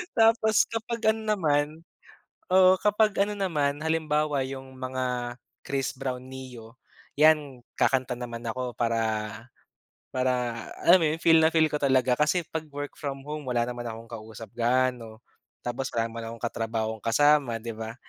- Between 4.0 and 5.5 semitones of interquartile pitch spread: Yes, average, 4.7 semitones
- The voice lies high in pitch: No, low, 130 Hz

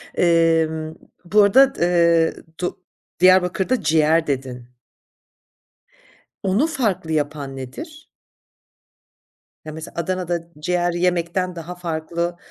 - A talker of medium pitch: Yes, medium, 170 Hz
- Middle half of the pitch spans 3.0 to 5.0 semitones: No, narrow, 2.5 semitones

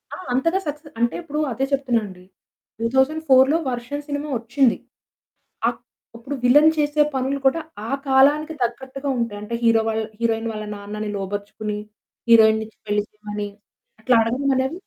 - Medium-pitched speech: No, high, 245 Hz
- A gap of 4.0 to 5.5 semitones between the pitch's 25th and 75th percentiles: Yes, average, 4.3 semitones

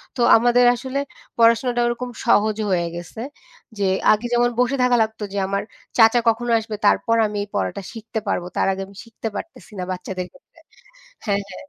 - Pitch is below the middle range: No, high, 225 Hz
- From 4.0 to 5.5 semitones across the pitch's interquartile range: No, average, 3.2 semitones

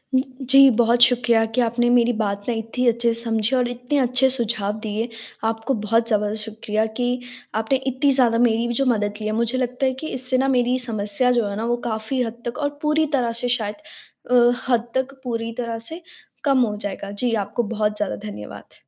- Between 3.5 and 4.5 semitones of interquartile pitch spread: No, narrow, 2.5 semitones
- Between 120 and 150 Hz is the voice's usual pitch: No, high, 235 Hz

